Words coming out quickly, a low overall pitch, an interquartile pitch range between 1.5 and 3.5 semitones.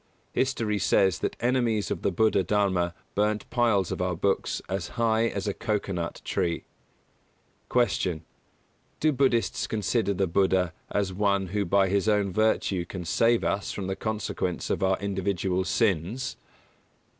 No: average, 155 wpm; low, 100 Hz; average, 2.9 semitones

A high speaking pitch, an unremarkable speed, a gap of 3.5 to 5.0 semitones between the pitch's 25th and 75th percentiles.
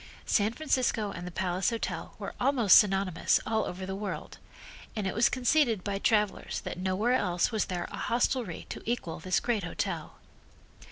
Yes: high, 205 Hz; average, 170 wpm; average, 4.2 semitones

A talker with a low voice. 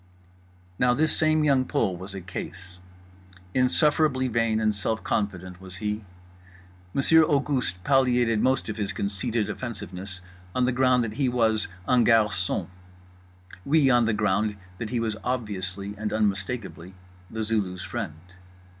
Yes: low, 110 Hz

